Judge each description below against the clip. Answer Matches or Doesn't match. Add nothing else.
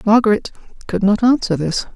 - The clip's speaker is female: Matches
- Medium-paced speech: Matches